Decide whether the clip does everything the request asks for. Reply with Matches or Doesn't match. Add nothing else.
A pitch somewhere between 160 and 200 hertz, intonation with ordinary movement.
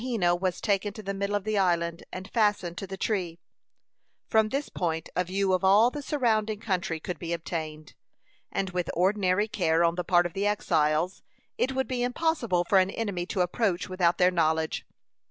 Matches